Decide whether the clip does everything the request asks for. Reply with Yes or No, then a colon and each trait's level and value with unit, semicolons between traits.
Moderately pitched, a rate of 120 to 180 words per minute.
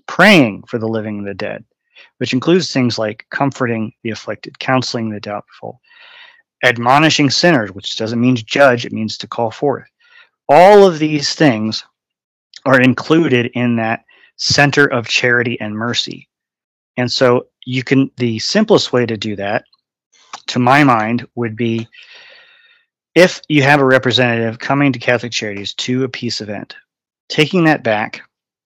No: low, 125 Hz; average, 155 wpm